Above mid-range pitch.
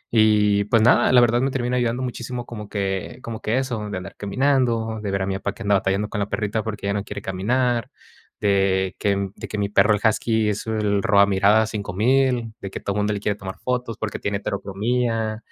No: low, 105 Hz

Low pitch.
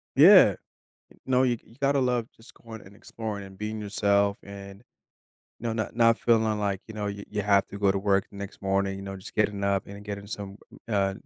Yes: low, 100 Hz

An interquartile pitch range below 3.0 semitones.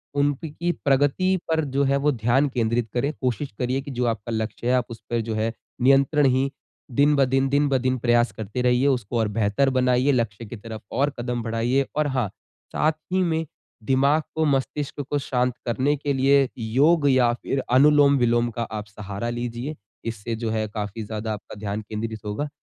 No: average, 3.5 semitones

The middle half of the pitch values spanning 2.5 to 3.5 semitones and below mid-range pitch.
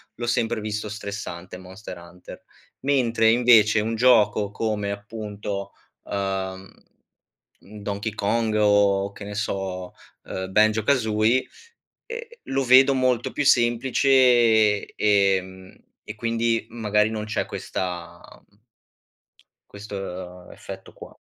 Yes: average, 2.8 semitones; low, 105 Hz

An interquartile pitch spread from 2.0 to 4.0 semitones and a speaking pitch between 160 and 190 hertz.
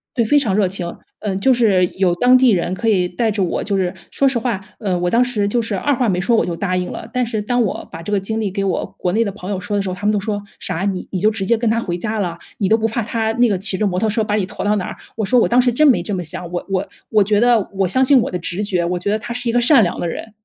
No: average, 3.7 semitones; high, 205 Hz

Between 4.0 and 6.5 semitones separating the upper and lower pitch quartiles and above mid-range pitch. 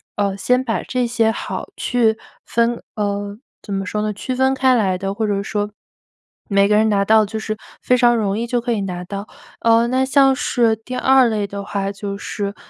No: average, 3.1 semitones; high, 220 Hz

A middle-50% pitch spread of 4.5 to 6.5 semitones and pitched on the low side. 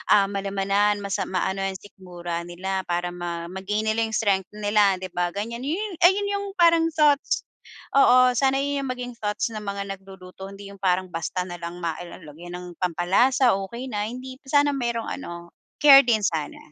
No: wide, 5.5 semitones; high, 200 Hz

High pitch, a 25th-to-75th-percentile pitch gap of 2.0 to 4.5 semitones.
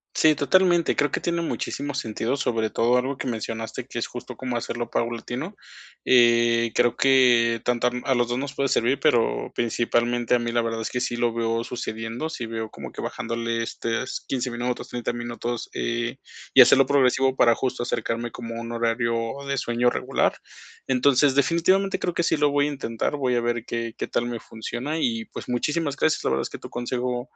No: low, 120 Hz; narrow, 2.5 semitones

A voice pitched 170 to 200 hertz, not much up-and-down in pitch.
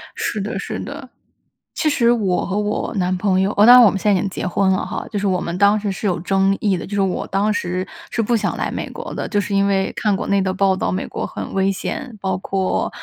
Yes: high, 195 Hz; narrow, 1.7 semitones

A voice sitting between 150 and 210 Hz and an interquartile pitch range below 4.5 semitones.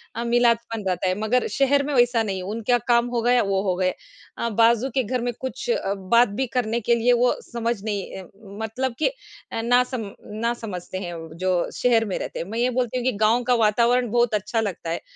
No: high, 235 Hz; average, 2.8 semitones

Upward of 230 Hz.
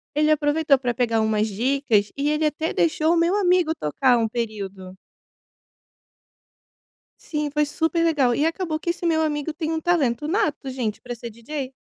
Yes: very high, 295 Hz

